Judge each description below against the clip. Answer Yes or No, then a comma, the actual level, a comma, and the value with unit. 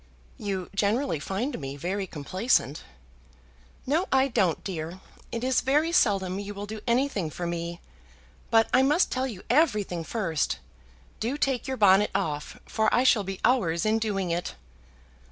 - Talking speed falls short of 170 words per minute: Yes, average, 155 wpm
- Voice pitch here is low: No, high, 205 Hz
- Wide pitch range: Yes, wide, 6.0 semitones